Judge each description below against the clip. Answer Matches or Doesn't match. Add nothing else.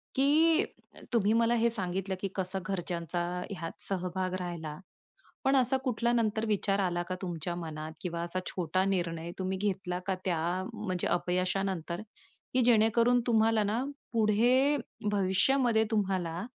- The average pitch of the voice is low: Doesn't match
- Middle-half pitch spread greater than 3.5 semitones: Matches